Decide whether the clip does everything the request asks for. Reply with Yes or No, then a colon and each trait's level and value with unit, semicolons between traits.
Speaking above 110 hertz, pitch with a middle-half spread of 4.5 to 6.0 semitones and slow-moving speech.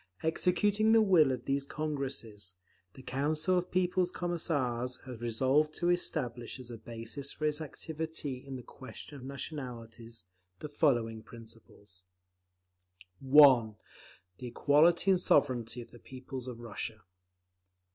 Yes: low, 135 Hz; average, 4.8 semitones; slow, 130 wpm